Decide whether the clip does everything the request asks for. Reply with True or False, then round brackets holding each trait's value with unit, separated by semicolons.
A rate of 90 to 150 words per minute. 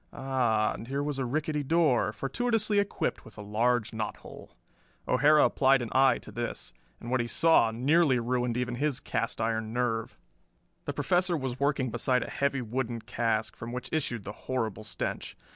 False (175 wpm)